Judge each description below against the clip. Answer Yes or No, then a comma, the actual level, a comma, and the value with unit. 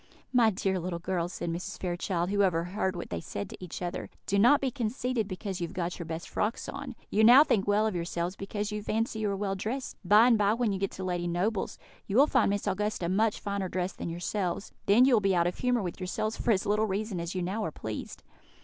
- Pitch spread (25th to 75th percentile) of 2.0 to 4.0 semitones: Yes, average, 3.4 semitones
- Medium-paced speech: No, fast, 250 wpm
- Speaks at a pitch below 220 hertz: Yes, high, 195 Hz